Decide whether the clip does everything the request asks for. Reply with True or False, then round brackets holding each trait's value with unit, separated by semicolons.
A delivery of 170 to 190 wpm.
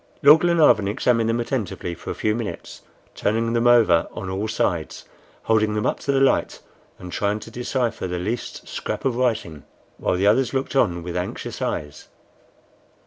True (175 wpm)